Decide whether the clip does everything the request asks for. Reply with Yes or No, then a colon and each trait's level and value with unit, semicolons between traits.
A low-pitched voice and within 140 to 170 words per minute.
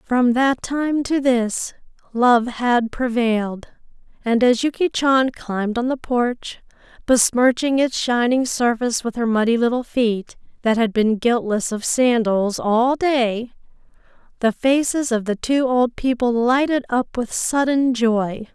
No: high, 245 Hz; average, 145 wpm